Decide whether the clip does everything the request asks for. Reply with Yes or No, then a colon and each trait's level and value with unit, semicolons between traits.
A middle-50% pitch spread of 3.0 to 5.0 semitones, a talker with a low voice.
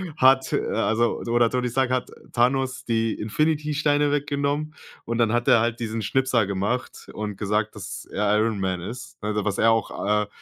Yes: average, 3.8 semitones; low, 115 Hz